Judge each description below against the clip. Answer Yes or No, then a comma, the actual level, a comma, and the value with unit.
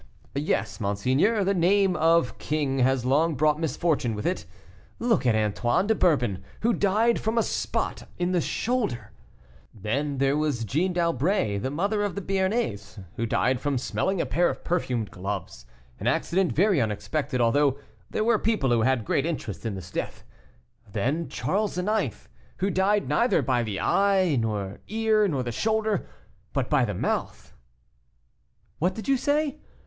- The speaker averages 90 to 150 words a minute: No, average, 165 wpm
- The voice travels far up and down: Yes, wide, 8.7 semitones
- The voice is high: No, medium, 150 Hz